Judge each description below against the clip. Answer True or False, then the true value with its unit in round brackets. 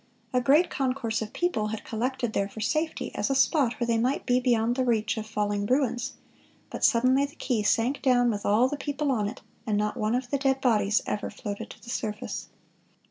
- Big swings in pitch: False (3.6 semitones)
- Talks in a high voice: True (240 Hz)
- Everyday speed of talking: False (215 wpm)